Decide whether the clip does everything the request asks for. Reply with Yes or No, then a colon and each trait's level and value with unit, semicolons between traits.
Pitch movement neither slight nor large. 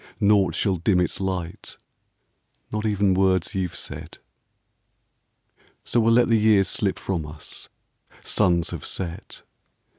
Yes: average, 3.0 semitones